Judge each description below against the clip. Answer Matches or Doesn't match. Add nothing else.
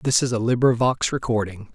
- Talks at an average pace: Matches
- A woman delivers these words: Doesn't match